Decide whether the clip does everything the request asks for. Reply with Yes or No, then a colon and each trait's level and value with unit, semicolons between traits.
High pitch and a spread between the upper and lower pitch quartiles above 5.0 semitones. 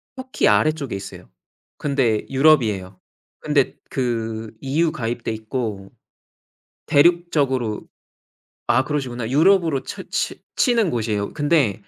No: low, 130 Hz; wide, 5.5 semitones